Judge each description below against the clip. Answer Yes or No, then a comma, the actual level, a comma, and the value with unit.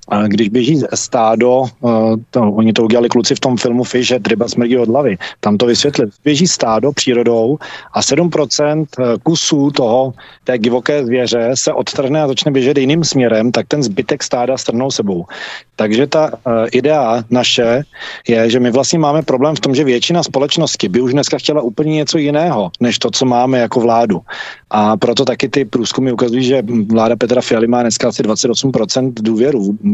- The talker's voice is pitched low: Yes, low, 125 Hz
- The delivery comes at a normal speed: No, fast, 175 wpm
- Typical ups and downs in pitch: Yes, average, 3.4 semitones